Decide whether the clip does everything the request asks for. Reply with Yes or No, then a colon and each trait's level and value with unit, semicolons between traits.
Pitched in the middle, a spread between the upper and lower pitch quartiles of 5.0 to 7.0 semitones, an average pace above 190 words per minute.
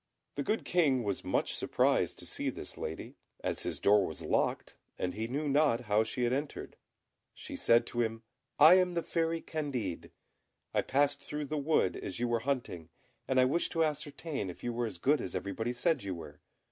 No: low, 130 Hz; average, 5.3 semitones; average, 200 wpm